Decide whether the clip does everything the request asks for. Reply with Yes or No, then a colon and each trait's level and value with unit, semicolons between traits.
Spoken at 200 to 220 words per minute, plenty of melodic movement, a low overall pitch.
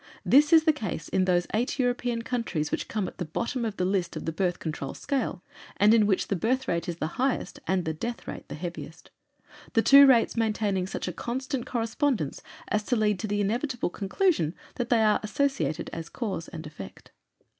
No: fast, 205 wpm; wide, 5.7 semitones; high, 215 Hz